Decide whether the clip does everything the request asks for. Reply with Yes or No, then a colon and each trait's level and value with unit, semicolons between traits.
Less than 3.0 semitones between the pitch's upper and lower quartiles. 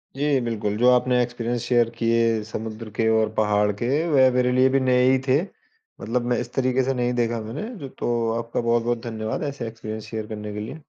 Yes: narrow, 2.4 semitones